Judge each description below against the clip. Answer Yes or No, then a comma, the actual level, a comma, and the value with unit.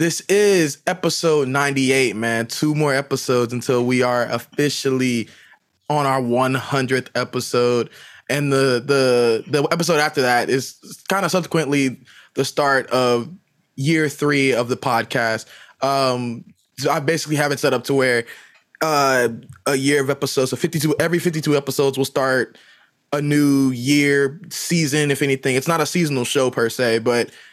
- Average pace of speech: Yes, average, 155 wpm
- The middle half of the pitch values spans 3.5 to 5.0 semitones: No, average, 2.8 semitones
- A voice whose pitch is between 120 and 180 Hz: Yes, low, 135 Hz